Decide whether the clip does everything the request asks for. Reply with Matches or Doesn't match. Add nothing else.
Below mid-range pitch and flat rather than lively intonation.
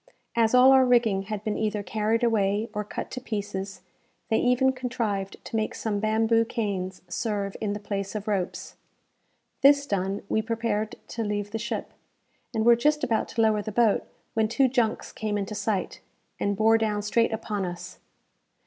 Doesn't match